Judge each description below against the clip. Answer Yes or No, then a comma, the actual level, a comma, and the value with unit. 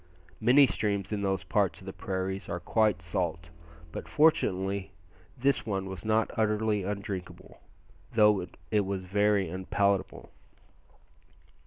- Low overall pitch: Yes, low, 100 Hz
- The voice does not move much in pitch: Yes, narrow, 2.2 semitones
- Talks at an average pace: No, slow, 125 wpm